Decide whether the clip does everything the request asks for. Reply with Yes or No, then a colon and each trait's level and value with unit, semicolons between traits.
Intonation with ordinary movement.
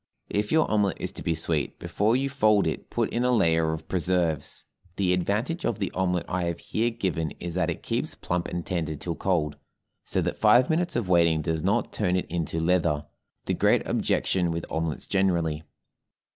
Yes: average, 4.2 semitones